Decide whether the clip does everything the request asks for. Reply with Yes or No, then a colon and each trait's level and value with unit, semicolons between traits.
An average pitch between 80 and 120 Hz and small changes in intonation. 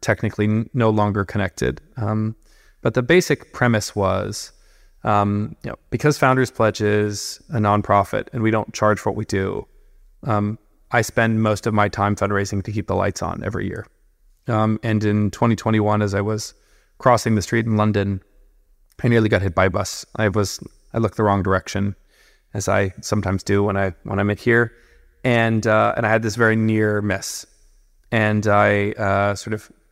Yes: low, 105 Hz; narrow, 1.7 semitones